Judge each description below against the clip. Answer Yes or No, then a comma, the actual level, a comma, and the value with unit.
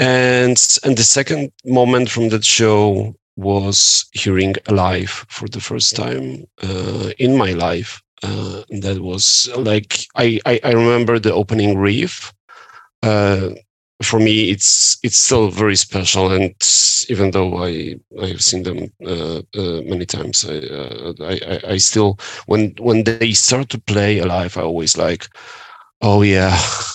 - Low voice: Yes, low, 105 Hz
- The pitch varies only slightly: No, average, 3.5 semitones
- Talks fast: No, average, 150 wpm